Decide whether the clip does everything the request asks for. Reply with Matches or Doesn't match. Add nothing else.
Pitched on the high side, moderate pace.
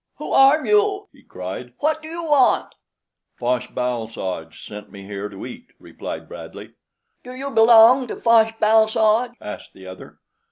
Matches